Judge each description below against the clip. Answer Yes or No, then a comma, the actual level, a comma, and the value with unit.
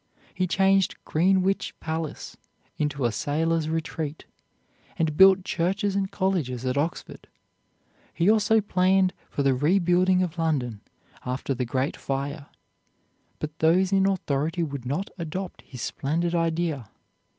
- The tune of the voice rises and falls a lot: No, average, 4.7 semitones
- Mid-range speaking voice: Yes, medium, 165 Hz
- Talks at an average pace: No, slow, 130 wpm